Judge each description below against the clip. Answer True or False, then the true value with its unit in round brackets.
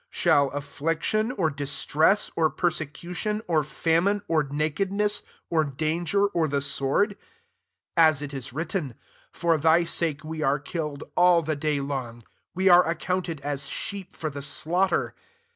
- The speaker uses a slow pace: False (160 wpm)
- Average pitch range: True (3.7 semitones)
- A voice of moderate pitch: True (160 Hz)